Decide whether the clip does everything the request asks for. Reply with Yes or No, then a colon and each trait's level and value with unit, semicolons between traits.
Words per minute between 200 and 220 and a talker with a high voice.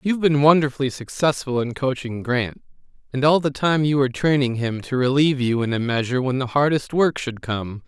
No: fast, 205 wpm; low, 135 Hz